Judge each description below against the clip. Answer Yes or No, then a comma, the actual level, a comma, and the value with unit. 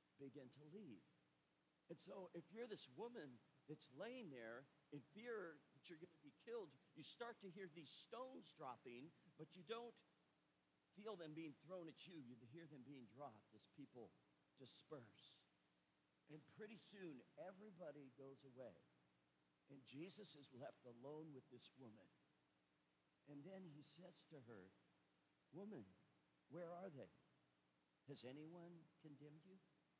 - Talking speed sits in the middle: Yes, average, 145 wpm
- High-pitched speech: No, medium, 150 Hz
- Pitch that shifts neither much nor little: No, wide, 6.0 semitones